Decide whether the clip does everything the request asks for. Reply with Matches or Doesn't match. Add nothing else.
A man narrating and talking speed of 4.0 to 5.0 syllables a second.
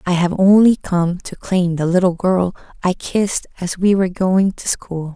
Doesn't match